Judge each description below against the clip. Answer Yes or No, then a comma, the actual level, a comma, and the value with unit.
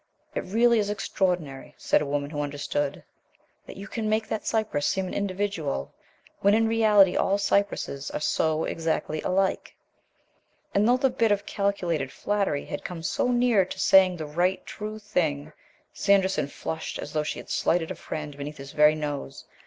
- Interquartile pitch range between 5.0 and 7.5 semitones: Yes, wide, 5.4 semitones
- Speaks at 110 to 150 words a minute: No, average, 175 wpm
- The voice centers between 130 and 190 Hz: Yes, medium, 185 Hz